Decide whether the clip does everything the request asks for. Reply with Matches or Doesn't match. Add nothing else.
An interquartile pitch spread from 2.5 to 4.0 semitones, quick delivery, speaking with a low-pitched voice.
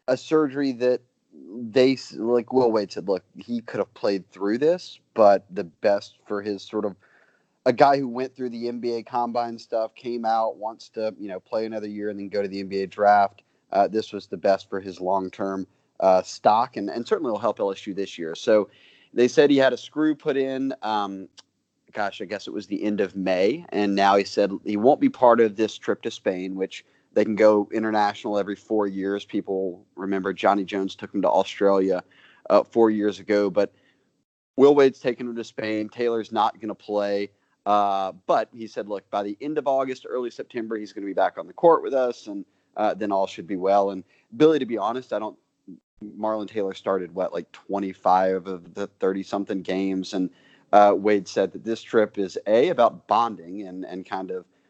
Matches